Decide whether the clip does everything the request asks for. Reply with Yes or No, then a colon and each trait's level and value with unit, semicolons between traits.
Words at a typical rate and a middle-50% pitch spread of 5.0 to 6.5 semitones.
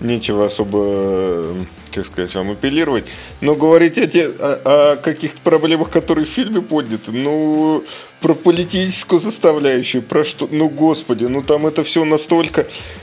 Yes: average, 145 wpm; wide, 5.5 semitones